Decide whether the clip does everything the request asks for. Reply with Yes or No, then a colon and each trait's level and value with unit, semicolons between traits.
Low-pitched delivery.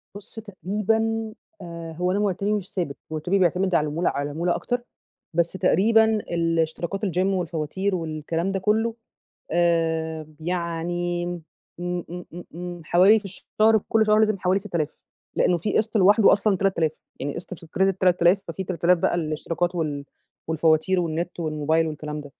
No: medium, 175 Hz